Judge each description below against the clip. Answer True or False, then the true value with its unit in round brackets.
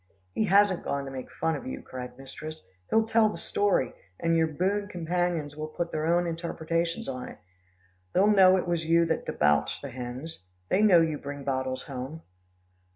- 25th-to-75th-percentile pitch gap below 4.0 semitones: False (4.5 semitones)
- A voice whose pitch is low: False (160 Hz)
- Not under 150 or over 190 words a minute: True (185 wpm)